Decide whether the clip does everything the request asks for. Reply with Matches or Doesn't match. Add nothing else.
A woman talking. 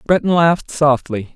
Doesn't match